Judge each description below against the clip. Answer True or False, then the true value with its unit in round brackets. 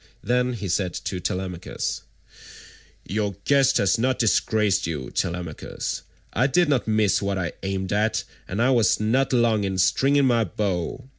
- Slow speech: False (155 wpm)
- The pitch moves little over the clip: False (4.9 semitones)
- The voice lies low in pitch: True (105 Hz)